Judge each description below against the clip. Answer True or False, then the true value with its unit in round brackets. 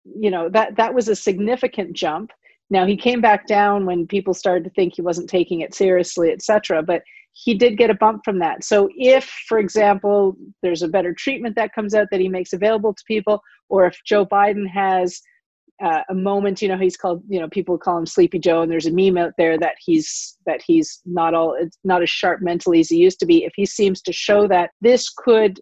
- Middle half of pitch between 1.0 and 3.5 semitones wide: False (3.9 semitones)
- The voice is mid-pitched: False (200 Hz)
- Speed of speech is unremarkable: False (230 wpm)